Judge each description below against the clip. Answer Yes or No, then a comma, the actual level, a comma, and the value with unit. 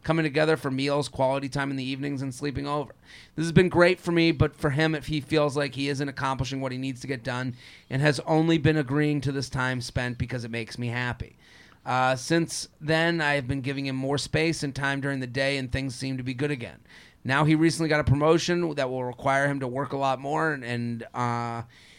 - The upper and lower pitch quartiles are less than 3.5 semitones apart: Yes, average, 2.8 semitones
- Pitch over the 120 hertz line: Yes, medium, 140 Hz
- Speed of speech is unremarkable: No, fast, 240 wpm